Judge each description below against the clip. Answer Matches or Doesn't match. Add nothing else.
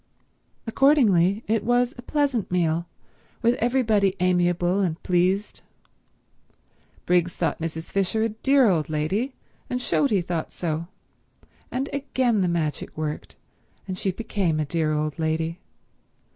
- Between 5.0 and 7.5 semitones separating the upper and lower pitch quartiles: Matches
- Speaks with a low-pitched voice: Doesn't match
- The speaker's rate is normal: Doesn't match